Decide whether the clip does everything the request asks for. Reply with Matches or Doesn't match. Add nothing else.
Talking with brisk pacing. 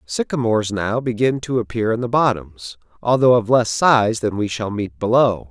Doesn't match